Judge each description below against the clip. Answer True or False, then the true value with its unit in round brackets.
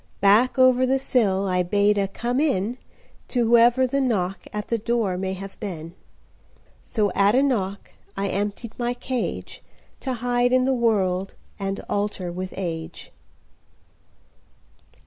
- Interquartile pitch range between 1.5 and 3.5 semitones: False (4.2 semitones)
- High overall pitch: True (210 Hz)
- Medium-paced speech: False (115 wpm)